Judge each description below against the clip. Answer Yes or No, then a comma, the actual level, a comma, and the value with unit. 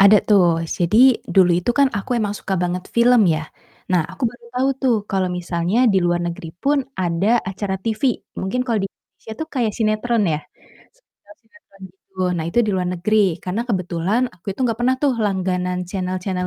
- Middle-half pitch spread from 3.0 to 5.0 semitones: Yes, average, 4.2 semitones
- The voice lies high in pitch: Yes, high, 195 Hz